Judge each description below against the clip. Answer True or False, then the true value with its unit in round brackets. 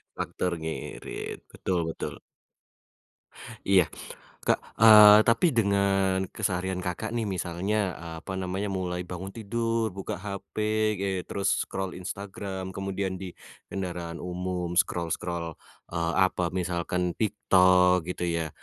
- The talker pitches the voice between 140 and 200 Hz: False (95 Hz)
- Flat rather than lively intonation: True (2.0 semitones)